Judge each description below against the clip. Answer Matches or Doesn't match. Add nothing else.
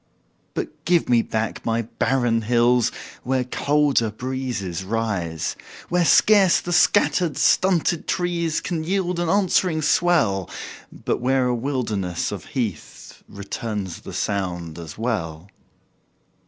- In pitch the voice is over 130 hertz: Doesn't match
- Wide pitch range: Matches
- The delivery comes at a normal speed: Doesn't match